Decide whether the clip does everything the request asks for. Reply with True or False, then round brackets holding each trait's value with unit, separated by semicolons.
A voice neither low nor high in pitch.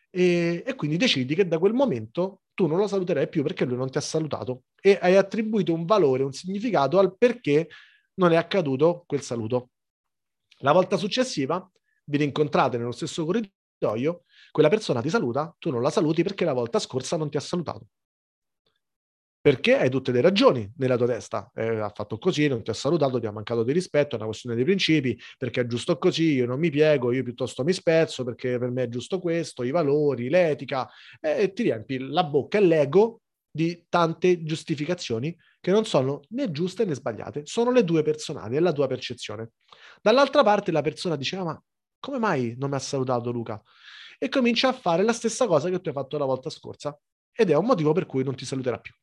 True (155 Hz)